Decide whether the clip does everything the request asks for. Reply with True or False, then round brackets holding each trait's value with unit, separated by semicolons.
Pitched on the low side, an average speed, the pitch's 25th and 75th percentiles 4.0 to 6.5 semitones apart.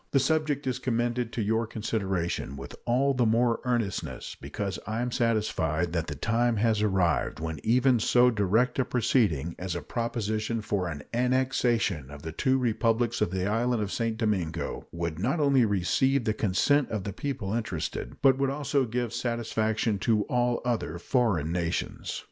True (115 Hz; 170 wpm; 4.6 semitones)